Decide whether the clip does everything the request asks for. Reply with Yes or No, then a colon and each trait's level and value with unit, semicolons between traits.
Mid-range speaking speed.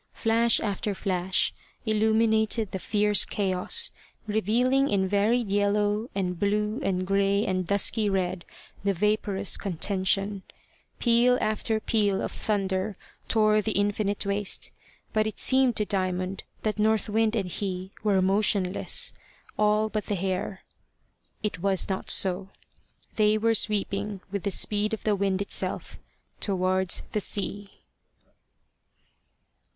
No: slow, 125 wpm